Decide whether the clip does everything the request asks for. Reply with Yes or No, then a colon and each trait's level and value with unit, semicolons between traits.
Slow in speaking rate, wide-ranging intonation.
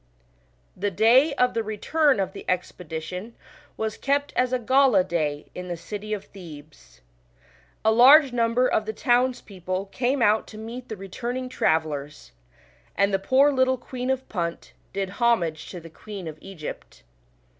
No: average, 160 wpm; wide, 5.7 semitones